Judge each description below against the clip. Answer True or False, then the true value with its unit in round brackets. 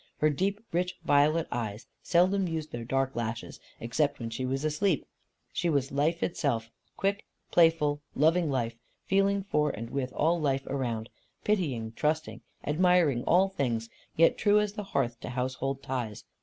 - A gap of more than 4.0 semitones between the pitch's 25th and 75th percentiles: True (5.6 semitones)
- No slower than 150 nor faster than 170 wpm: True (155 wpm)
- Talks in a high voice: False (145 Hz)